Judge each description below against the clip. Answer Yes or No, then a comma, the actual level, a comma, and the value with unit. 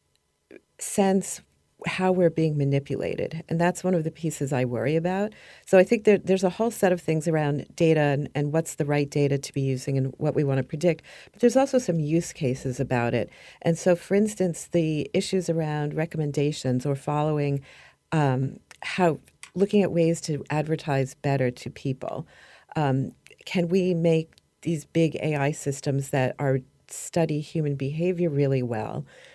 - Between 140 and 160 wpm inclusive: No, average, 170 wpm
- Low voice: No, medium, 155 Hz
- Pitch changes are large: No, average, 3.8 semitones